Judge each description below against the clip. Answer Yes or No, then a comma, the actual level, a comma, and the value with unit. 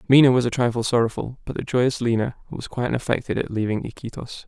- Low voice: Yes, low, 120 Hz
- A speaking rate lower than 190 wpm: No, average, 200 wpm